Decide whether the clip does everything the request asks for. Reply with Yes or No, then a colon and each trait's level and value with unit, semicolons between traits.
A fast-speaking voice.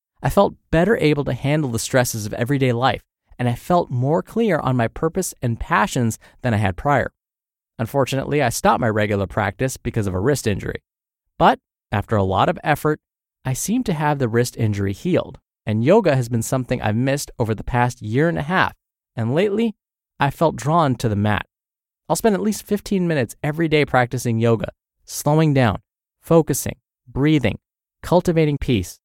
No: average, 180 wpm